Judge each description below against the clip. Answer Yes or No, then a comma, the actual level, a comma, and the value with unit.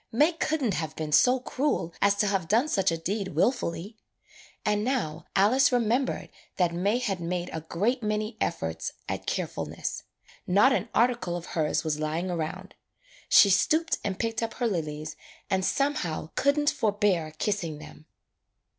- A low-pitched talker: No, high, 200 Hz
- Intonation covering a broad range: Yes, wide, 6.3 semitones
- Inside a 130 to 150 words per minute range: No, average, 165 wpm